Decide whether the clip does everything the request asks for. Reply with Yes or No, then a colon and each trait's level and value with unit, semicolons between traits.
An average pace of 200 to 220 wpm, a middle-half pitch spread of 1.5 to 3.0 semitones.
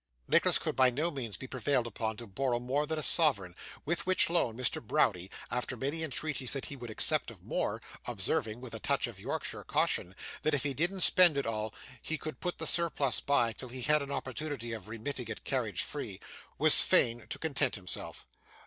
No: fast, 205 wpm; average, 4.7 semitones